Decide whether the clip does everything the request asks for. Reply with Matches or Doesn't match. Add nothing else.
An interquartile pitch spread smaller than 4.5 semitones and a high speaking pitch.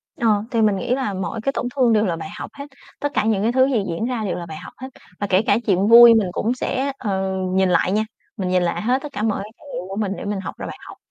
Matches